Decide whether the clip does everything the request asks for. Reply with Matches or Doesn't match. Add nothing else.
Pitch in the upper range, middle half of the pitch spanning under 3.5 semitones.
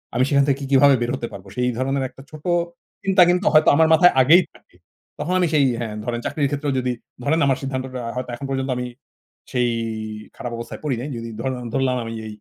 Doesn't match